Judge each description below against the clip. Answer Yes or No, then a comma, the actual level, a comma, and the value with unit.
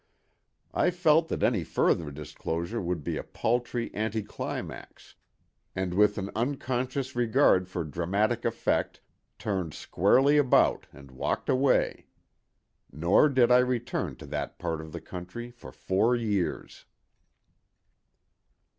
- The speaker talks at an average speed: No, slow, 125 wpm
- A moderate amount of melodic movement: No, wide, 5.9 semitones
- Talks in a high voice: No, low, 110 Hz